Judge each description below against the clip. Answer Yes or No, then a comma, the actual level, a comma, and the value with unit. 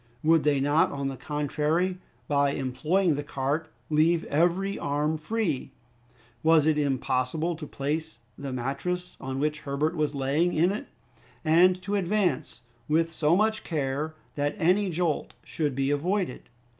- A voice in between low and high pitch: Yes, medium, 155 Hz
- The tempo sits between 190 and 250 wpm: No, average, 145 wpm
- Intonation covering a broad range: No, average, 3.6 semitones